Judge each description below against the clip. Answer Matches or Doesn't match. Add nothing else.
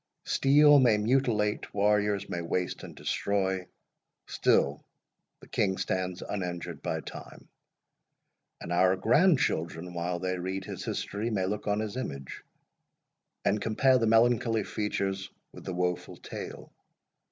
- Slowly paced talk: Matches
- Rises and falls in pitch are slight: Doesn't match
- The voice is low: Matches